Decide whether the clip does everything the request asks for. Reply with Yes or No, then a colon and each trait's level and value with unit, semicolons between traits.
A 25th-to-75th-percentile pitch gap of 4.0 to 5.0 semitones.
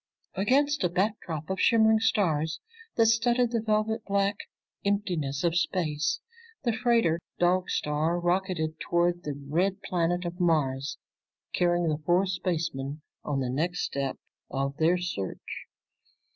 Yes: average, 4.4 semitones